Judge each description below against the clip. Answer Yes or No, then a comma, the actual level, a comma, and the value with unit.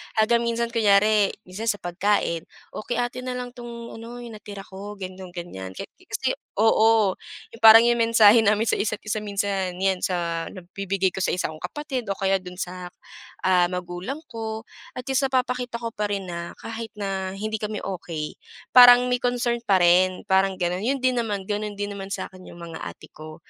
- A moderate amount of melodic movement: Yes, average, 3.8 semitones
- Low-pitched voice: No, high, 205 Hz